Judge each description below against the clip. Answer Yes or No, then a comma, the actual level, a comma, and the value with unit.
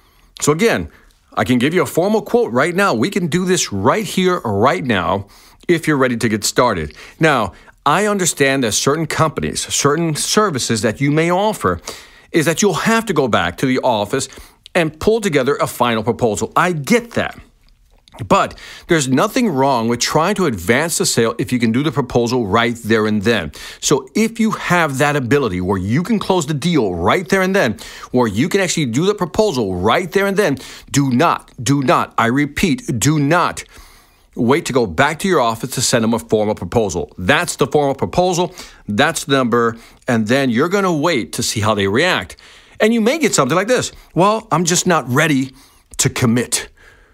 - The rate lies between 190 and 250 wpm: Yes, average, 200 wpm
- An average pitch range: No, wide, 7.2 semitones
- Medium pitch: Yes, medium, 150 Hz